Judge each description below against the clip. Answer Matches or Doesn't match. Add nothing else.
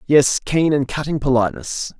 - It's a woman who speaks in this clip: Doesn't match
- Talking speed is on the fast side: Doesn't match